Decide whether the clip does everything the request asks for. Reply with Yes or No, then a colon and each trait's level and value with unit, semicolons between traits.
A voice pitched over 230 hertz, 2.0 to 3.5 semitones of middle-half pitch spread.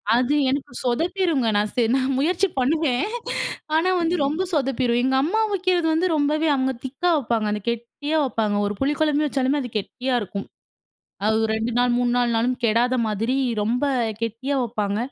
No: very high, 260 Hz; average, 4.2 semitones